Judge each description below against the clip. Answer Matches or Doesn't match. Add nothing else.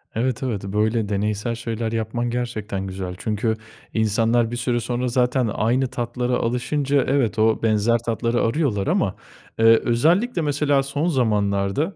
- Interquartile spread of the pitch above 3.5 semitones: Doesn't match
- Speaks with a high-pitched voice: Doesn't match